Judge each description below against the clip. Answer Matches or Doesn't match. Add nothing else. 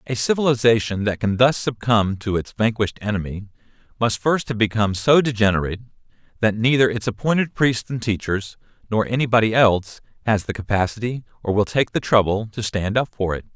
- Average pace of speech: Matches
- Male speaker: Matches